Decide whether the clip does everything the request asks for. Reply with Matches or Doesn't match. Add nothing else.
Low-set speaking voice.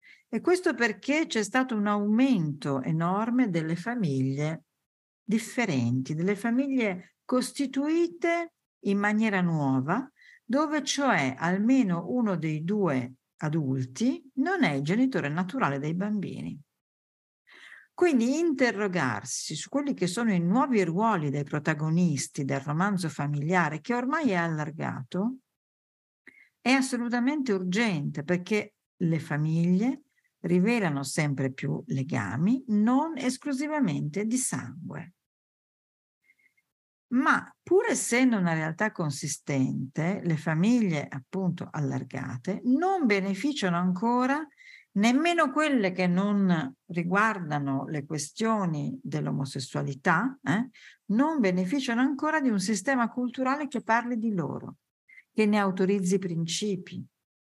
Doesn't match